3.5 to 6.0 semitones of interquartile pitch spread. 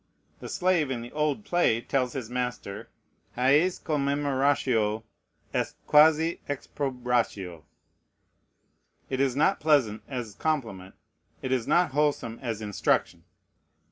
Yes: average, 4.3 semitones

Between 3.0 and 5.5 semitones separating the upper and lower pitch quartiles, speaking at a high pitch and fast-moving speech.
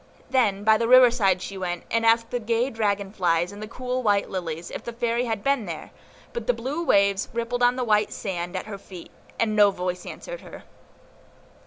Yes: average, 3.7 semitones; high, 215 Hz; fast, 210 wpm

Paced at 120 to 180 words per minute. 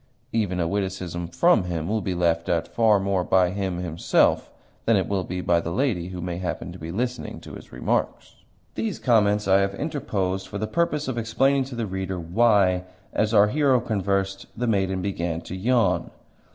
No: average, 190 wpm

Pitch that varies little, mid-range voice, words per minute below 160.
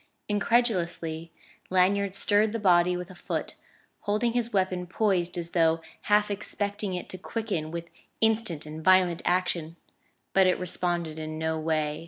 No: average, 3.5 semitones; medium, 180 Hz; average, 150 wpm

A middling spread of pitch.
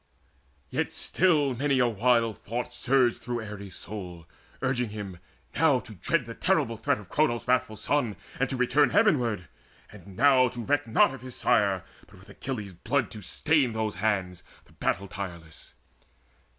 Yes: average, 4.5 semitones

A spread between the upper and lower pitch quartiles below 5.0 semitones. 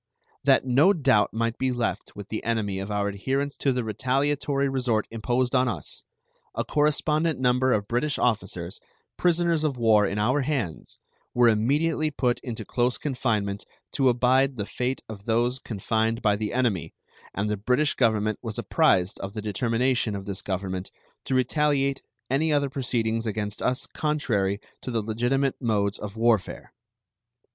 Yes: average, 4.2 semitones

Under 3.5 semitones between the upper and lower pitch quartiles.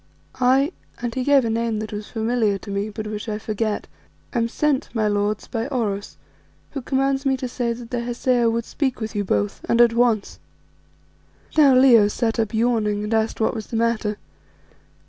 Yes: narrow, 2.6 semitones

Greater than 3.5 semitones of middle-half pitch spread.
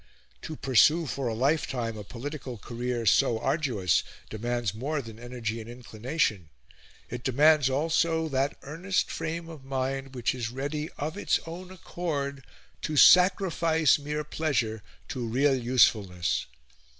Yes: average, 4.7 semitones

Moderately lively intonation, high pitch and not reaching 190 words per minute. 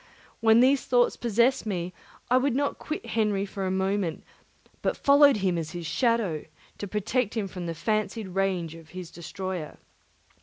Yes: average, 4.5 semitones; high, 200 Hz; average, 165 wpm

